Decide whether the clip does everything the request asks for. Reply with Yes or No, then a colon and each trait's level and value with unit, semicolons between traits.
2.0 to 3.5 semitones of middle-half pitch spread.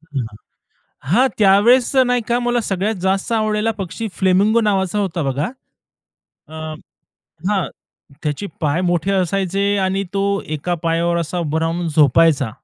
No: average, 4.0 semitones